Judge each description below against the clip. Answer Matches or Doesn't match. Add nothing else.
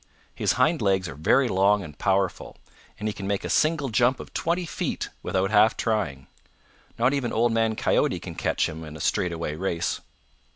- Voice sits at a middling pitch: Doesn't match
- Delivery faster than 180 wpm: Matches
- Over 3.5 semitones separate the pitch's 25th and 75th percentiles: Matches